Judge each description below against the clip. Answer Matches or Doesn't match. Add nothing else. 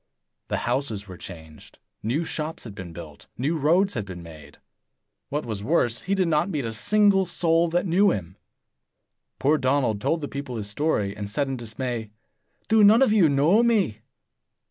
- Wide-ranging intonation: Matches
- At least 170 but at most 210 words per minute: Matches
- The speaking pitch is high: Doesn't match